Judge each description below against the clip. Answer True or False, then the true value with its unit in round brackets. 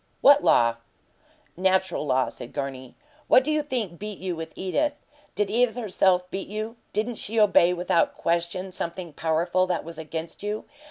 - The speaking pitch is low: False (185 Hz)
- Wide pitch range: False (4.2 semitones)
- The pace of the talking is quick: False (165 wpm)